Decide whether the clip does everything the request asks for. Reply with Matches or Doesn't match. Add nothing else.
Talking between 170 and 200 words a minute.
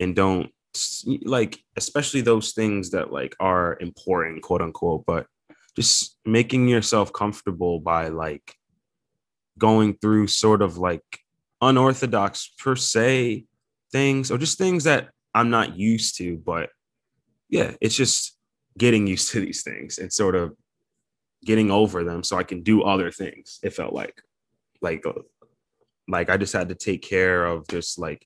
Doesn't match